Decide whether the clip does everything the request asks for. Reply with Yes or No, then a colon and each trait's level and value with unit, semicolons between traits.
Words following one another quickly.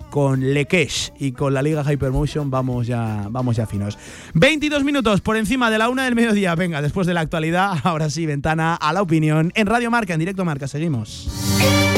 Yes: fast, 195 wpm